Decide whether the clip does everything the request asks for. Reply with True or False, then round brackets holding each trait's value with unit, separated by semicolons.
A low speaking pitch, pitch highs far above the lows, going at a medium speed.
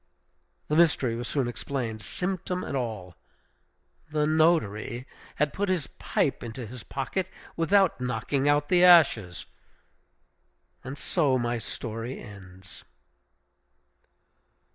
False (130 Hz; 5.8 semitones; 110 wpm)